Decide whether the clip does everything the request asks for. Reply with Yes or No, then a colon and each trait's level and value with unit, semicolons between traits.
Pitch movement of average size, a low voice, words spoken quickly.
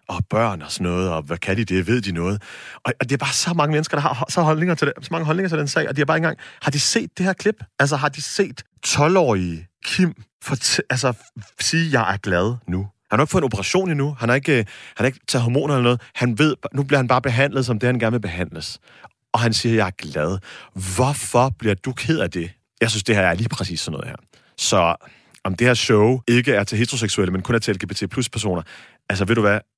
No: wide, 6.3 semitones; low, 120 Hz; fast, 265 wpm